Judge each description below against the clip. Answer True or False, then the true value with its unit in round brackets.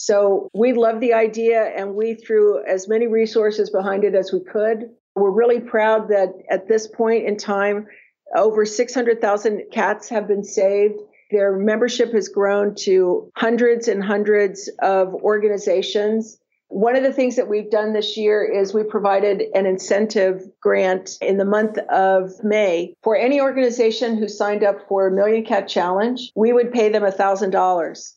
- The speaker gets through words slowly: False (165 wpm)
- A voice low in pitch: False (210 Hz)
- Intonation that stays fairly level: True (2.1 semitones)